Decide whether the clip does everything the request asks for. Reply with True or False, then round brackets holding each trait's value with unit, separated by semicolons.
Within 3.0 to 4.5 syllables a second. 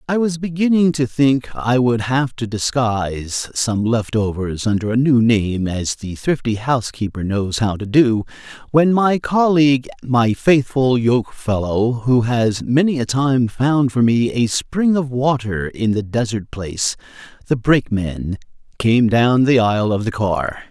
True (4.1 syllables/s)